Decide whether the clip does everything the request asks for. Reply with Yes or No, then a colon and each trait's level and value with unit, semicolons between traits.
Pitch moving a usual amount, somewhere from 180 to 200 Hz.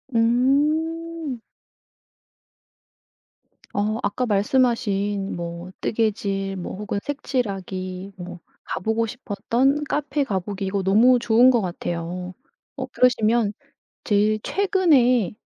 No: average, 4.6 semitones; high, 220 Hz